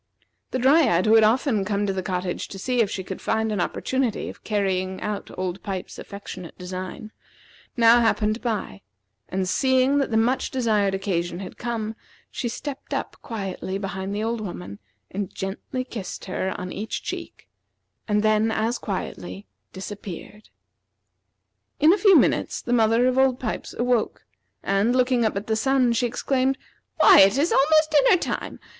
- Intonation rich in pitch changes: No, average, 4.5 semitones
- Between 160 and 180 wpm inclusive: Yes, average, 165 wpm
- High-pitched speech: Yes, high, 215 Hz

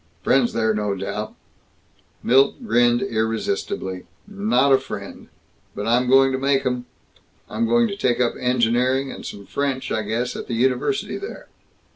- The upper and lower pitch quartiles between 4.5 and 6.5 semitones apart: No, average, 3.0 semitones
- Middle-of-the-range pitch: No, low, 125 Hz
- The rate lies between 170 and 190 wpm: No, average, 155 wpm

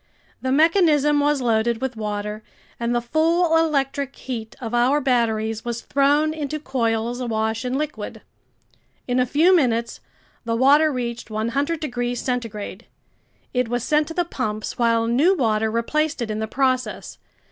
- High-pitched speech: Yes, very high, 250 Hz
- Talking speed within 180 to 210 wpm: No, average, 155 wpm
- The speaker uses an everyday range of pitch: Yes, average, 4.3 semitones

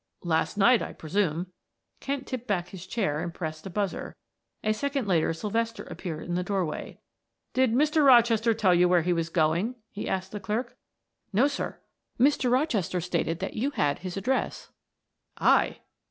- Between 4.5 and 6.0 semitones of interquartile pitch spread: Yes, wide, 5.5 semitones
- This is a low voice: No, high, 195 Hz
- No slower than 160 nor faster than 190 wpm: Yes, average, 170 wpm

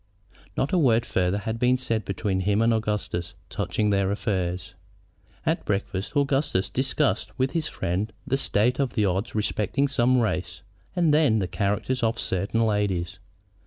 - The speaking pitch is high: No, low, 110 Hz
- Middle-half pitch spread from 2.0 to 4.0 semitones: No, average, 4.7 semitones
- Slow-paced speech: No, average, 160 wpm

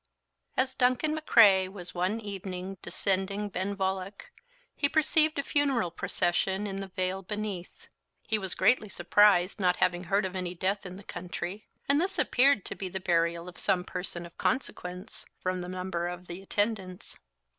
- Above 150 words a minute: Yes, average, 165 wpm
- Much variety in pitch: No, average, 2.7 semitones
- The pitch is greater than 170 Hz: Yes, high, 190 Hz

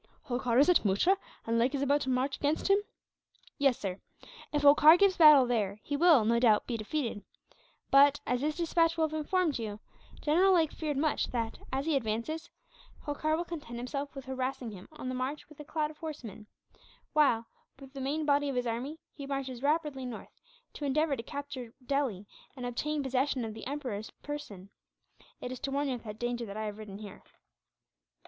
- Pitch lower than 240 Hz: No, very high, 275 Hz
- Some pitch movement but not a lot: Yes, average, 4.2 semitones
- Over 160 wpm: Yes, average, 195 wpm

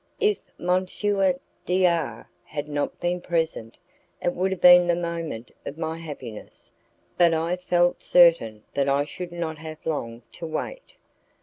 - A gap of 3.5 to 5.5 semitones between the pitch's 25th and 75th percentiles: No, average, 3.0 semitones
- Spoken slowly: No, average, 150 wpm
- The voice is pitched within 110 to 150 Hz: No, medium, 165 Hz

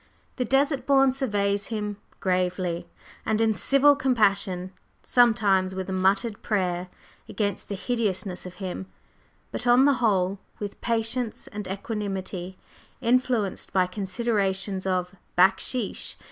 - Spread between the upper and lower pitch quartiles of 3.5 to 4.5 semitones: Yes, average, 3.9 semitones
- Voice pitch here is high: Yes, high, 200 Hz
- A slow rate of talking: Yes, slow, 120 wpm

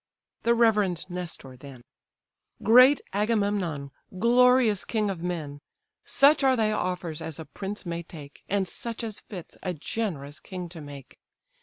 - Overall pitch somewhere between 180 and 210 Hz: Yes, medium, 185 Hz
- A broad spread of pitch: Yes, wide, 5.7 semitones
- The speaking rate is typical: Yes, average, 145 wpm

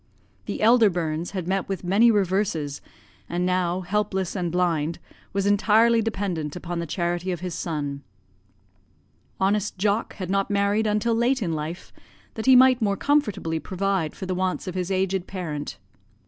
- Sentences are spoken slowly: No, average, 160 wpm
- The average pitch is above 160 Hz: Yes, high, 190 Hz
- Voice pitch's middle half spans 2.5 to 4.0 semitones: Yes, average, 3.2 semitones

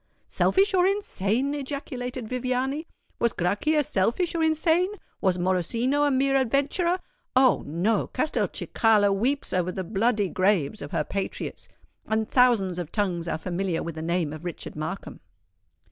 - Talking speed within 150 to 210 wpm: No, average, 140 wpm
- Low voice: No, high, 225 Hz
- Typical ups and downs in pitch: No, wide, 7.1 semitones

